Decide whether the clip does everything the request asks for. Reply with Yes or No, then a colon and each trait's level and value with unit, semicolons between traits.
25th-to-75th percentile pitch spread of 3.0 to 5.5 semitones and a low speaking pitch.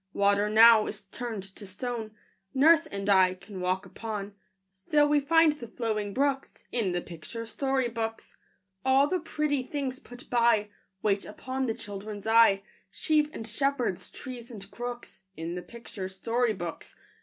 No: average, 4.5 semitones; high, 225 Hz